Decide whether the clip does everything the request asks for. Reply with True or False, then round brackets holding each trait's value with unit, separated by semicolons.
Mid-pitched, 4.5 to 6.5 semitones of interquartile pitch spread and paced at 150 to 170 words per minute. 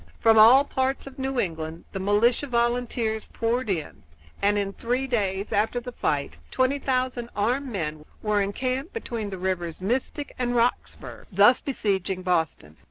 False (225 Hz; 4.8 semitones; 160 wpm)